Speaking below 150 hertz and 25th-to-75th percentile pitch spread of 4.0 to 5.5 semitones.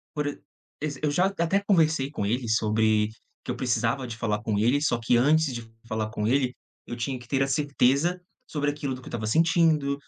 Yes: low, 135 Hz; average, 4.5 semitones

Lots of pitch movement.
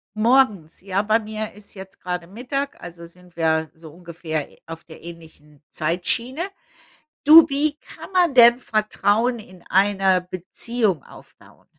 Yes: wide, 5.8 semitones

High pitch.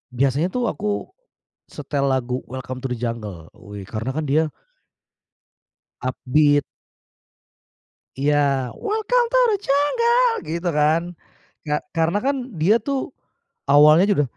No: medium, 155 Hz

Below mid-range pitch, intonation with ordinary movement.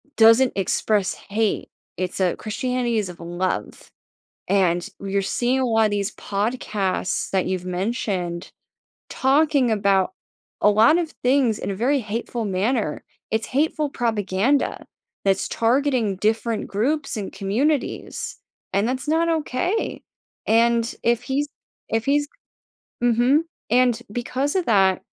No: high, 225 Hz; average, 4.8 semitones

